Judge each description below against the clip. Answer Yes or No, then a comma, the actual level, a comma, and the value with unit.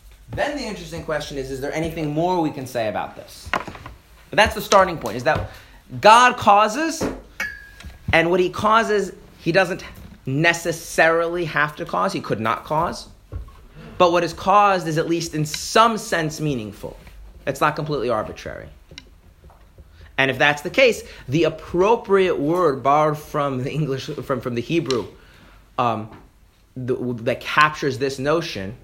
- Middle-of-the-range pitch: Yes, medium, 155 Hz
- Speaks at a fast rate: No, average, 155 wpm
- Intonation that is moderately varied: No, wide, 5.9 semitones